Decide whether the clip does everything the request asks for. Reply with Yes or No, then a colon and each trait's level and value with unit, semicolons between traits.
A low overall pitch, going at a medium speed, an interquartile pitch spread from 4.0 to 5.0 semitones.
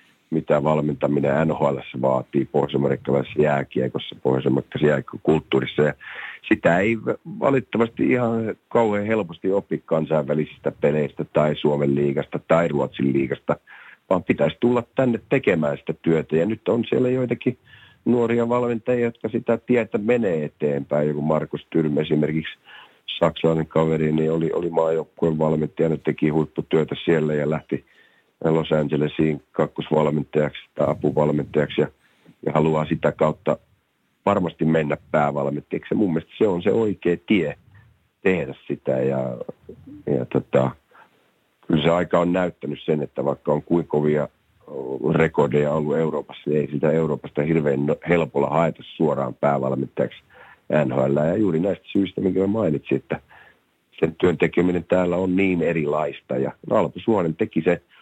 Yes: very low, 80 Hz; average, 130 wpm; average, 4.3 semitones